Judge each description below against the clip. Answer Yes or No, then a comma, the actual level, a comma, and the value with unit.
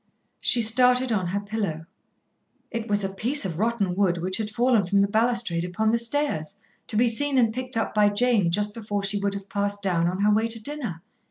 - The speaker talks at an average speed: No, fast, 220 wpm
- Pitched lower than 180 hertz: No, high, 210 Hz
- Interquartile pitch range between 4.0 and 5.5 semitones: No, average, 3.0 semitones